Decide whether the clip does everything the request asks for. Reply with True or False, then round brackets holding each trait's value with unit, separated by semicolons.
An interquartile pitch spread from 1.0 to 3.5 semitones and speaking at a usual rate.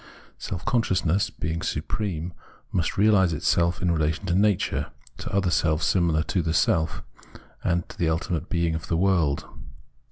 True (2.6 semitones; 155 wpm)